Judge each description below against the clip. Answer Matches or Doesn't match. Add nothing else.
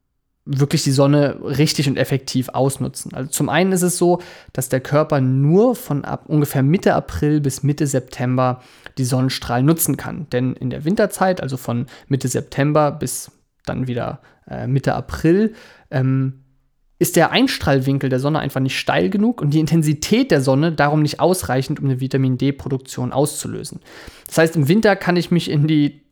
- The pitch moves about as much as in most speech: Matches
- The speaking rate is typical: Matches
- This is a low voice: Doesn't match